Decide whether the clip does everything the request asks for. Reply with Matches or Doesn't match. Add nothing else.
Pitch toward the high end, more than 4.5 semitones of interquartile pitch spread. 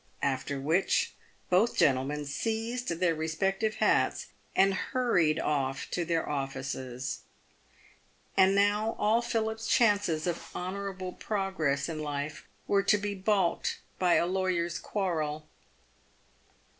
Doesn't match